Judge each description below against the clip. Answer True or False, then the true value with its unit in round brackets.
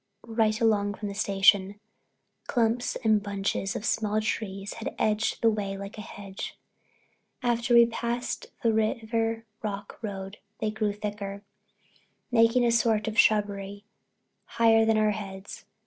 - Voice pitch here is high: True (215 Hz)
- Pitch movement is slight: True (2.0 semitones)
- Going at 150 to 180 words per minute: False (140 wpm)